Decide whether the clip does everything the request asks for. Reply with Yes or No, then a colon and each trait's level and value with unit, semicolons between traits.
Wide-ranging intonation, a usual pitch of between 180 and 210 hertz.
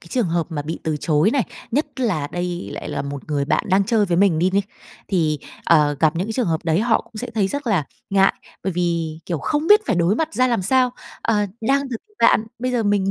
Yes: wide, 5.9 semitones; high, 190 Hz